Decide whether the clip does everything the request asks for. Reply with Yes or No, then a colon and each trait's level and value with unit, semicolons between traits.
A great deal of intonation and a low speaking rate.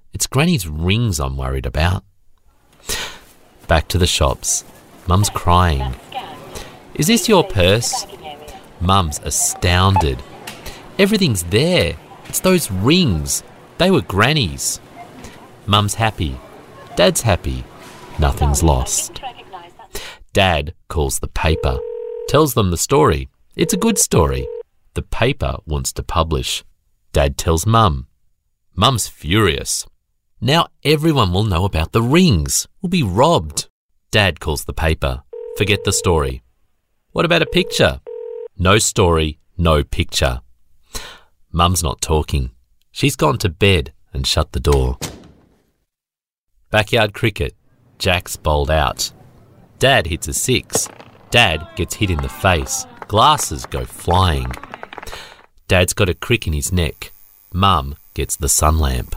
Yes: wide, 7.2 semitones; slow, 120 wpm